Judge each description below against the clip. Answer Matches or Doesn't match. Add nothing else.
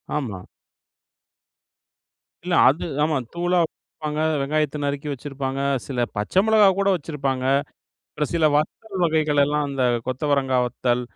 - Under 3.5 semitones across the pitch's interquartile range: Matches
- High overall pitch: Doesn't match